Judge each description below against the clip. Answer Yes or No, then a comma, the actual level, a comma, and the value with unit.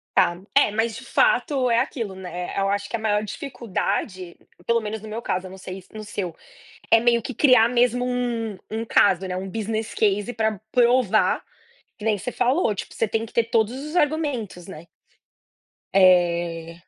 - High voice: Yes, high, 220 Hz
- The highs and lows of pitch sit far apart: No, average, 3.9 semitones